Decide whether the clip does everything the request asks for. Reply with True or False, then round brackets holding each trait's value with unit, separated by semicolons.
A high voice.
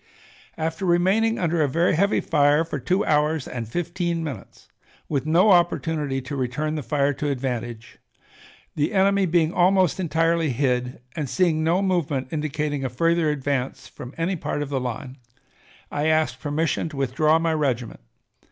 False (155 Hz)